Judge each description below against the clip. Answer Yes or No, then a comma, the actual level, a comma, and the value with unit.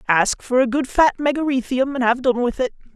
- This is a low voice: No, very high, 255 Hz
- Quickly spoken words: Yes, fast, 225 wpm